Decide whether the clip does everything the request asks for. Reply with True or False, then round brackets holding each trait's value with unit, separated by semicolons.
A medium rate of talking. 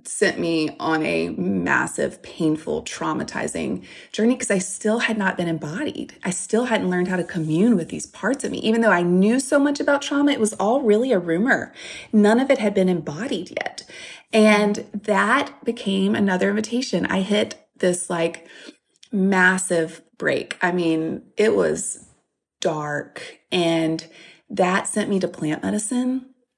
True (160 wpm)